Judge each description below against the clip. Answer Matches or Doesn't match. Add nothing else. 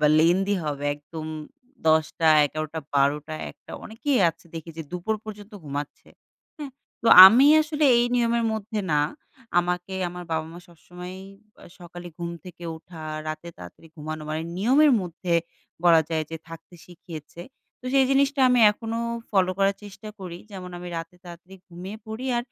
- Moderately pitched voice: Matches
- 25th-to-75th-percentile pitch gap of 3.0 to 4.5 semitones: Doesn't match